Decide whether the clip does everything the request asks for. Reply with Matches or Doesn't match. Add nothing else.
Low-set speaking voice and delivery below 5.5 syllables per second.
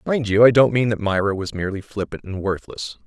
Doesn't match